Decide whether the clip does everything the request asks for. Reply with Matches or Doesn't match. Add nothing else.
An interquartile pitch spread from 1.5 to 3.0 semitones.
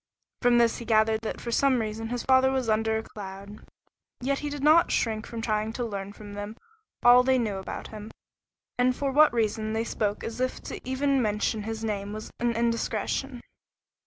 Matches